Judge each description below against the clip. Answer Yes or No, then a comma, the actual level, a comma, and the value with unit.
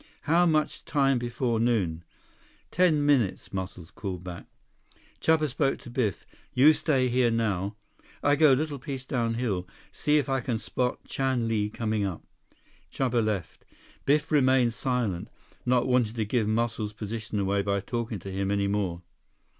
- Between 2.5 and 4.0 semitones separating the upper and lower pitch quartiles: No, average, 4.6 semitones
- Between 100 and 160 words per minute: Yes, average, 155 wpm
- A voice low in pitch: Yes, low, 120 Hz